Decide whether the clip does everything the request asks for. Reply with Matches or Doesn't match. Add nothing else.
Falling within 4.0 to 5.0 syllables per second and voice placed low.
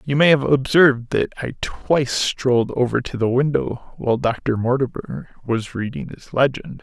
Matches